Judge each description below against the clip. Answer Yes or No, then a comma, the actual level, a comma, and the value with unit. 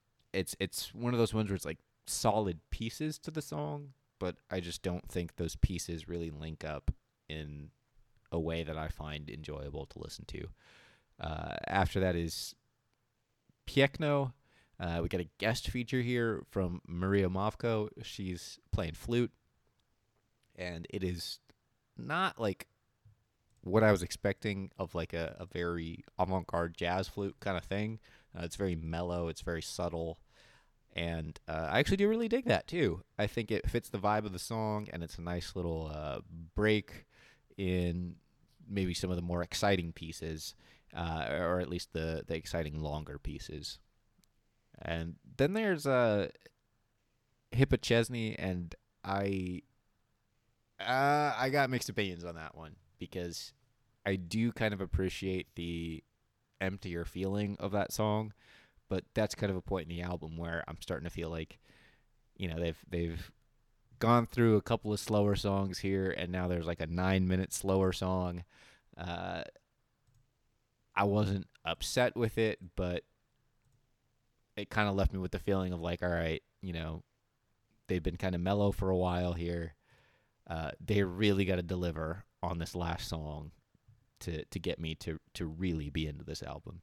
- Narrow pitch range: No, average, 4.6 semitones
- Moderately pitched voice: No, very low, 95 Hz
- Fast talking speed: No, average, 165 wpm